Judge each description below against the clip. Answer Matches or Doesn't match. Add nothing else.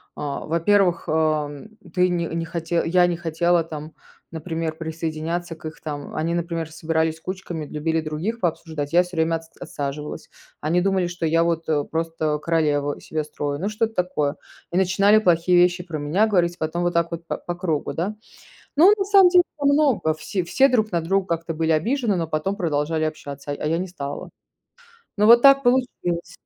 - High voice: Doesn't match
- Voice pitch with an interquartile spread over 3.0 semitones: Doesn't match